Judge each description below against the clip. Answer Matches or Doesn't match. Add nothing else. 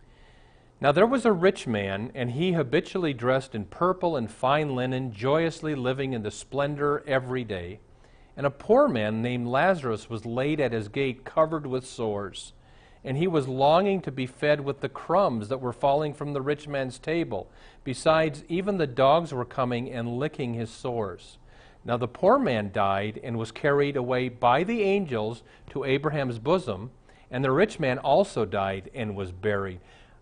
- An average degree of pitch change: Matches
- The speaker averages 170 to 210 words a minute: Matches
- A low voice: Matches